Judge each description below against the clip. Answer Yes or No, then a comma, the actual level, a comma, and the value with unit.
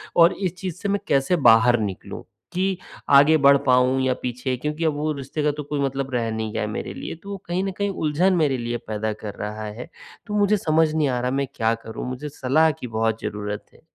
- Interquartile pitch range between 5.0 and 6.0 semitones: Yes, average, 5.3 semitones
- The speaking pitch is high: No, medium, 140 Hz